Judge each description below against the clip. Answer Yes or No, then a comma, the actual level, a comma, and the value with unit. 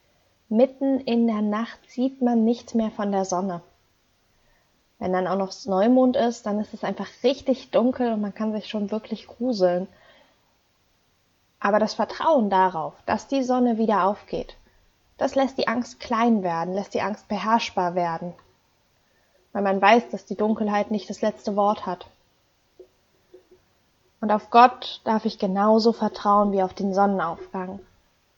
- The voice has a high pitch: Yes, high, 210 Hz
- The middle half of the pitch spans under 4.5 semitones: Yes, average, 3.7 semitones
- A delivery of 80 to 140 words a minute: No, average, 150 wpm